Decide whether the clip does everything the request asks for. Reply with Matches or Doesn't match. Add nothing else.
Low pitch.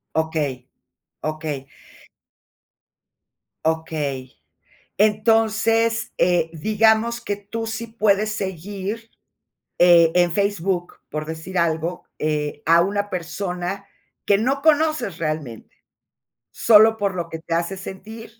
Doesn't match